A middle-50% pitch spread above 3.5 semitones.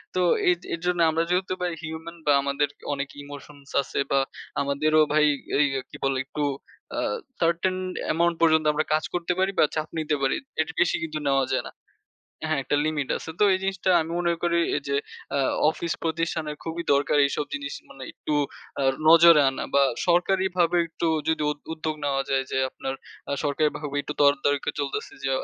No: average, 3.0 semitones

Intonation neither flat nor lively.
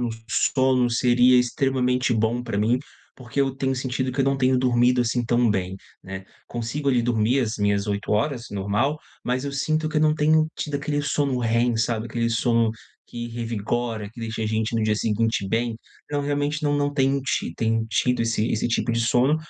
Yes: average, 3.1 semitones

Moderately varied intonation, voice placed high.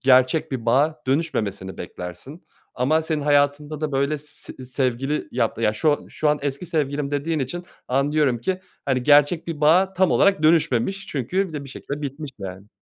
No: average, 3.2 semitones; medium, 145 Hz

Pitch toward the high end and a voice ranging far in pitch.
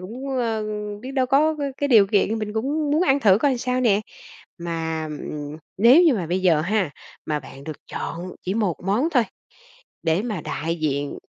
Yes: high, 210 Hz; wide, 7.4 semitones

